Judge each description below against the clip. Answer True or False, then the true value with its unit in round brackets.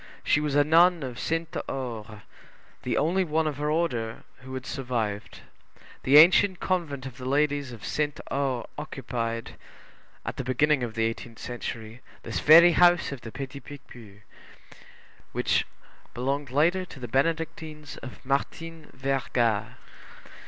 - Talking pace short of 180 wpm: True (145 wpm)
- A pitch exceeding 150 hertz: False (140 Hz)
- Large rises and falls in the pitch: False (4.3 semitones)